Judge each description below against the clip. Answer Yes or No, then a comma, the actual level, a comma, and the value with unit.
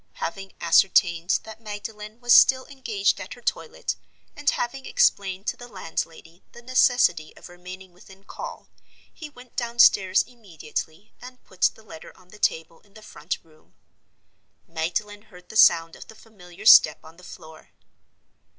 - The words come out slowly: No, average, 155 wpm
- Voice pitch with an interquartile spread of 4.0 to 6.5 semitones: Yes, wide, 5.4 semitones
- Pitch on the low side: No, high, 200 Hz